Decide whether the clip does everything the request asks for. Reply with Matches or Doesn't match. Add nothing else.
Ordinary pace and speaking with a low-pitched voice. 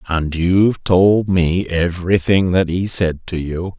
Matches